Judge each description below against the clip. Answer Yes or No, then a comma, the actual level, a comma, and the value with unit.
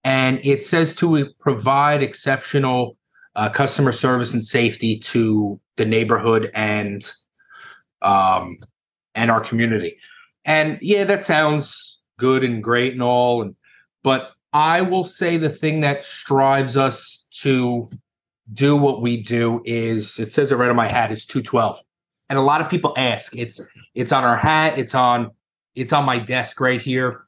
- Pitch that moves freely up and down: No, average, 3.7 semitones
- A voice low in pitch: Yes, low, 130 Hz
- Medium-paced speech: Yes, average, 155 wpm